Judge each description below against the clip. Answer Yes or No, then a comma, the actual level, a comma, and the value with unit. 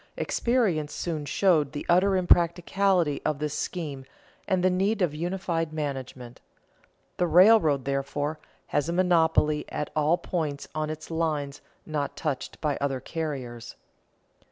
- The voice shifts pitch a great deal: No, average, 3.4 semitones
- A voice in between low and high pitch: Yes, medium, 155 Hz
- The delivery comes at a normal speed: No, slow, 130 wpm